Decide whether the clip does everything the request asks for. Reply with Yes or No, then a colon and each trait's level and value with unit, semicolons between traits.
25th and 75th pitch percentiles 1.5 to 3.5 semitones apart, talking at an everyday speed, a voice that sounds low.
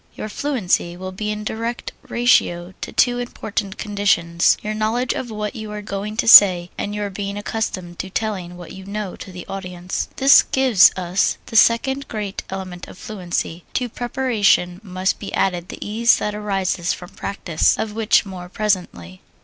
No: average, 3.2 semitones; average, 175 wpm; high, 200 Hz